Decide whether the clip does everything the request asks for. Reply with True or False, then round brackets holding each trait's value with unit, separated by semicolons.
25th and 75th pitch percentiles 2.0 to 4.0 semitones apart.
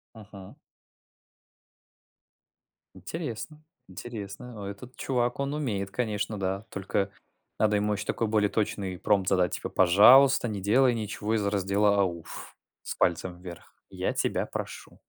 True (3.3 semitones)